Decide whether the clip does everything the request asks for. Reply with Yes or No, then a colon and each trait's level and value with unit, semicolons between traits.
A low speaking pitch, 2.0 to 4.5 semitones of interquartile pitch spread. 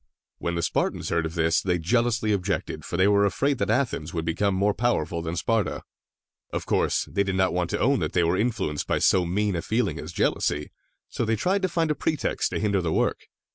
No: low, 100 Hz; average, 5.1 semitones